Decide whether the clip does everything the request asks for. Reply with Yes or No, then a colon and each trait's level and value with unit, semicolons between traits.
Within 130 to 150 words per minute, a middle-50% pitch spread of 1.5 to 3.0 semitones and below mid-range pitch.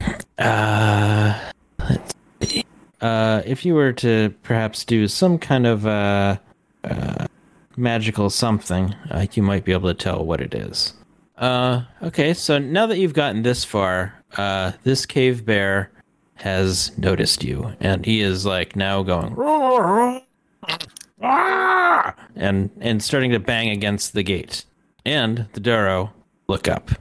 No: average, 140 wpm; average, 4.7 semitones; low, 110 Hz